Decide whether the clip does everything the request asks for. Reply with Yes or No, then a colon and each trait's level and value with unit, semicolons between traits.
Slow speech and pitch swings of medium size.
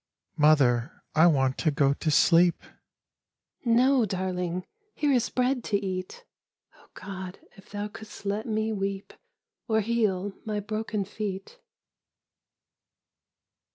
Yes: slow, 125 wpm; average, 3.5 semitones